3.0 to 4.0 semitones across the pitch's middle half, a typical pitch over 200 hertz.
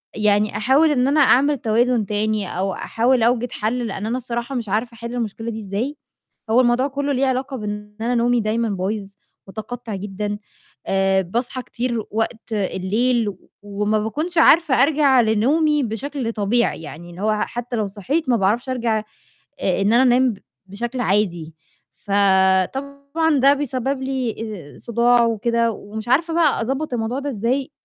Yes: average, 3.7 semitones; high, 235 Hz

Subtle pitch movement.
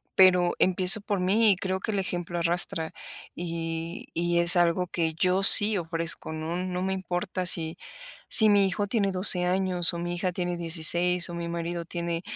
Yes: narrow, 1.8 semitones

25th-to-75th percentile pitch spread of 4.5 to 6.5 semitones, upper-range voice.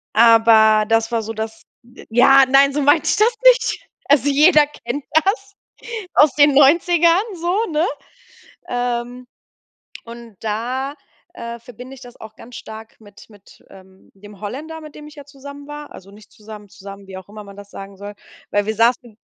Yes: average, 5.2 semitones; high, 240 Hz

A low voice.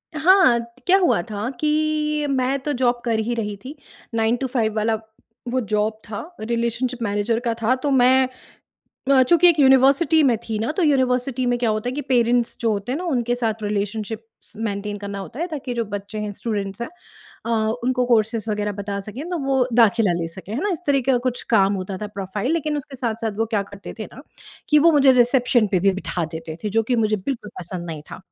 No: high, 235 Hz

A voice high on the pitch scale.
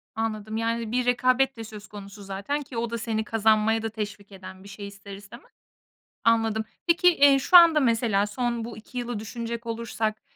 Yes: high, 225 Hz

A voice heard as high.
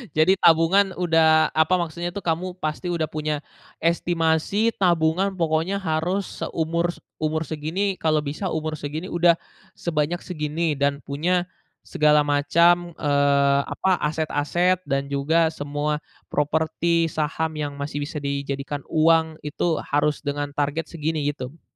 No: medium, 160 Hz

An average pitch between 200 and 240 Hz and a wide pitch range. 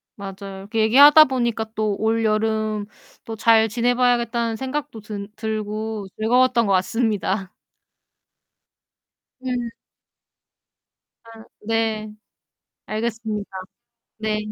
No: high, 220 Hz; narrow, 1.8 semitones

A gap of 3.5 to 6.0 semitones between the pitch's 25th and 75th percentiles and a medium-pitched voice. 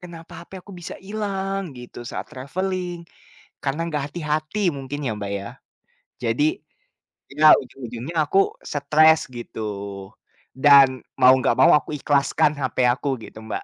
Yes: average, 4.6 semitones; medium, 145 Hz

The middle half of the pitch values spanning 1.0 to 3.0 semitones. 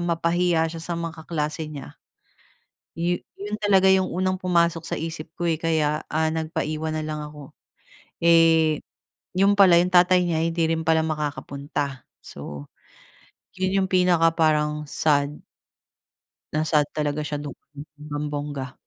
Yes: narrow, 2.4 semitones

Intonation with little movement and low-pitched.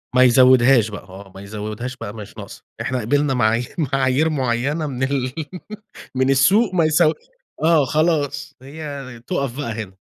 No: average, 3.8 semitones; low, 130 Hz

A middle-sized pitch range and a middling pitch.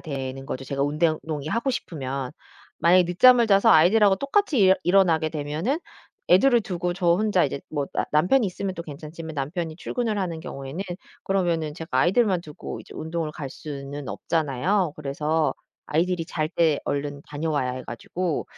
Yes: average, 4.2 semitones; medium, 160 Hz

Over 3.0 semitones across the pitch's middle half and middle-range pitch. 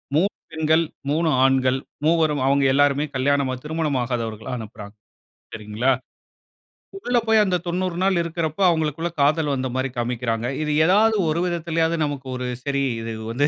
Yes: average, 4.3 semitones; medium, 145 Hz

